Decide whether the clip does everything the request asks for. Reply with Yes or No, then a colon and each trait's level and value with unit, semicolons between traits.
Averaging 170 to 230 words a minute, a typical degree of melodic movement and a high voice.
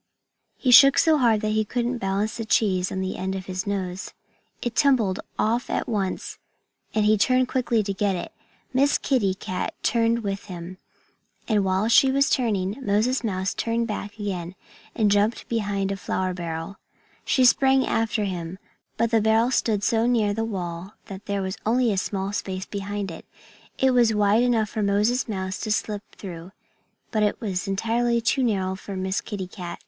Yes: average, 185 wpm; average, 3.4 semitones; high, 210 Hz